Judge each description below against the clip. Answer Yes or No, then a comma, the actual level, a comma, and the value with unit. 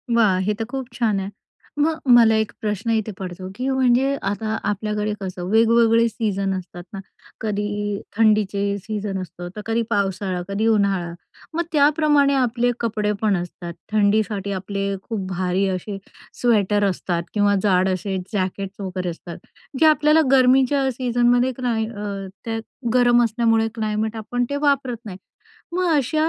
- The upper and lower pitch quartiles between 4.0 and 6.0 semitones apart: No, average, 3.5 semitones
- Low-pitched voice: No, high, 215 Hz